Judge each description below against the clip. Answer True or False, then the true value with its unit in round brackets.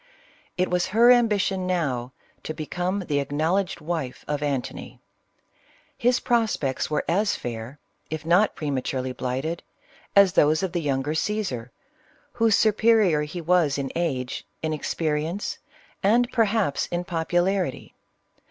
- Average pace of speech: False (130 wpm)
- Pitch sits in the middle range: True (170 Hz)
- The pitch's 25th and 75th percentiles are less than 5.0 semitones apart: False (5.5 semitones)